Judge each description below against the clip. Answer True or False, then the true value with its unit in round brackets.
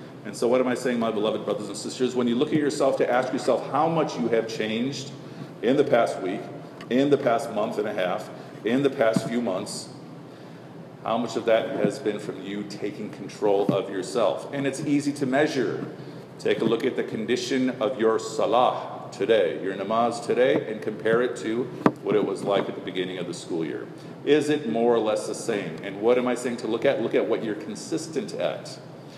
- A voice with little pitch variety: False (4.3 semitones)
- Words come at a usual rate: False (220 wpm)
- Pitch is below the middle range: True (130 Hz)